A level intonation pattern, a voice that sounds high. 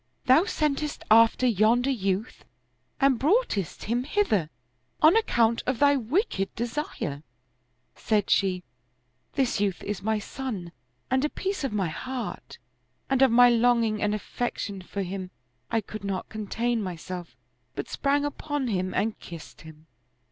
No: wide, 5.4 semitones; high, 225 Hz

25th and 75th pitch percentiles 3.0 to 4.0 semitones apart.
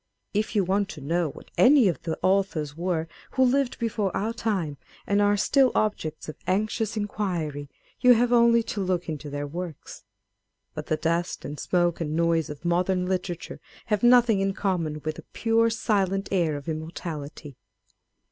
No: average, 5.0 semitones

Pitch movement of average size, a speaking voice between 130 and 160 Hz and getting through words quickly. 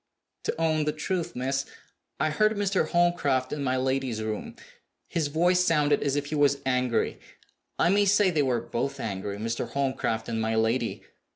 No: average, 4.6 semitones; medium, 140 Hz; average, 175 wpm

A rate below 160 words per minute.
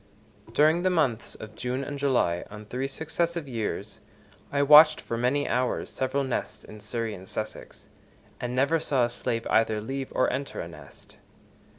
No: average, 170 wpm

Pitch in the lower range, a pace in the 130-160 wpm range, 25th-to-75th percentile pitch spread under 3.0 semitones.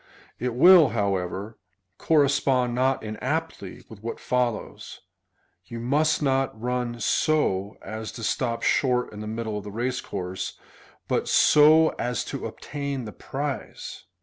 No: low, 125 Hz; average, 140 wpm; average, 4.3 semitones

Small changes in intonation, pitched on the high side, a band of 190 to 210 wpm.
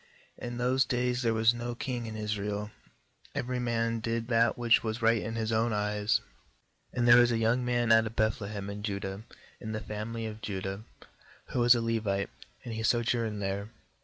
No: narrow, 2.0 semitones; low, 115 Hz; average, 200 wpm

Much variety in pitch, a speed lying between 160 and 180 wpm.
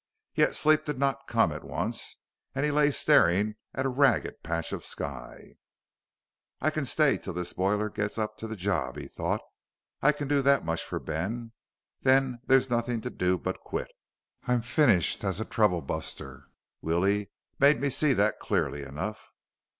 Yes: wide, 6.8 semitones; average, 170 wpm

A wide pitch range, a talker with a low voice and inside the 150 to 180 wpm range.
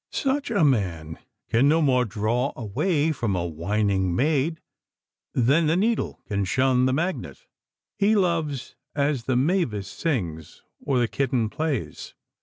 No: wide, 7.2 semitones; low, 130 Hz; average, 140 wpm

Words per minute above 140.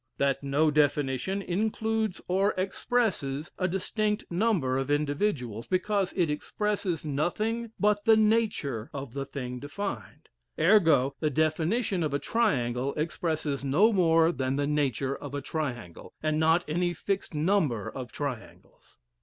No: slow, 135 wpm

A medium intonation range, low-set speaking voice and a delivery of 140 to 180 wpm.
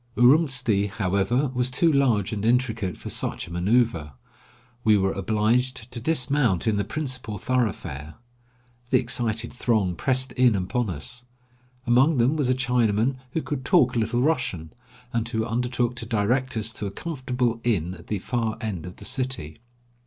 Yes: average, 3.8 semitones; low, 120 Hz; average, 165 wpm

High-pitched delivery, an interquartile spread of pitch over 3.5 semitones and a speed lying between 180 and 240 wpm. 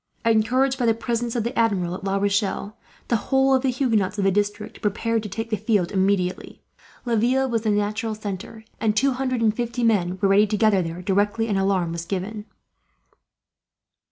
No: high, 215 Hz; average, 2.8 semitones; average, 190 wpm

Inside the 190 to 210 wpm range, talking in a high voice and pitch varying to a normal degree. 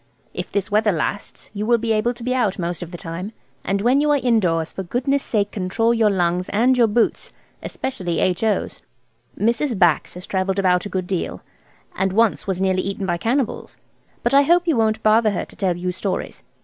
Yes: fast, 205 wpm; high, 205 Hz; average, 4.1 semitones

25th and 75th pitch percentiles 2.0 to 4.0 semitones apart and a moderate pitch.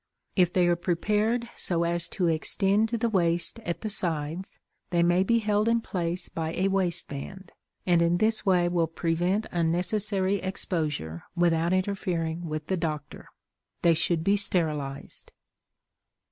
Yes: average, 2.7 semitones; medium, 175 Hz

